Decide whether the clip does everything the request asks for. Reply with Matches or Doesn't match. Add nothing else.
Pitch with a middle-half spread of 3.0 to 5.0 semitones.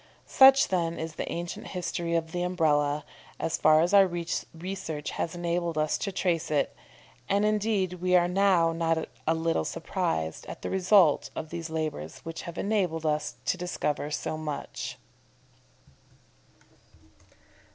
Doesn't match